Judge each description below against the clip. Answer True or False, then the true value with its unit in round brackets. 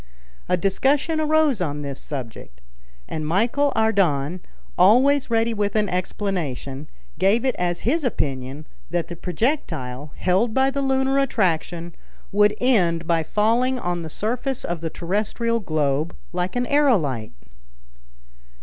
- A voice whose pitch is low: False (195 Hz)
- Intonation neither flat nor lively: False (7.2 semitones)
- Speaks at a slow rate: True (130 wpm)